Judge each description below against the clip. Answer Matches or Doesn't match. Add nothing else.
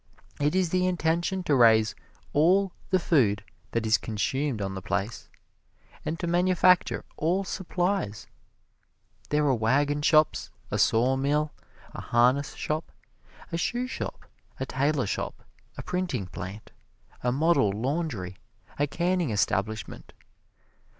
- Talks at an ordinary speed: Doesn't match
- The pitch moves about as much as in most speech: Doesn't match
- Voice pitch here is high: Doesn't match